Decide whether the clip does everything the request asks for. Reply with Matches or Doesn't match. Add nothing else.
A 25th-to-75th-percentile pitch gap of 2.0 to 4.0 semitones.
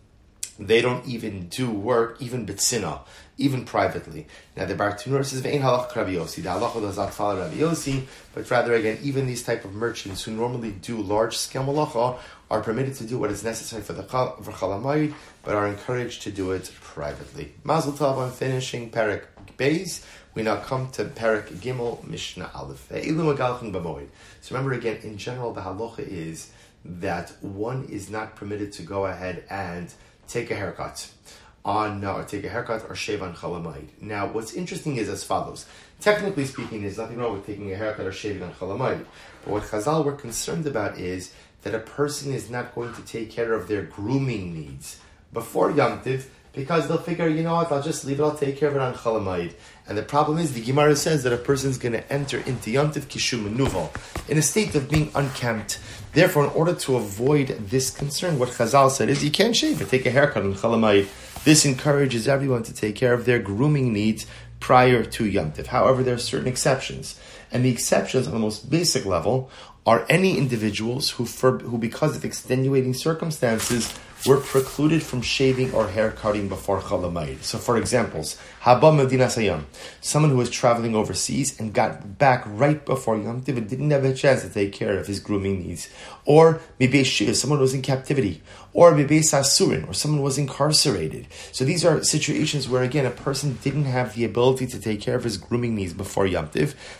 Doesn't match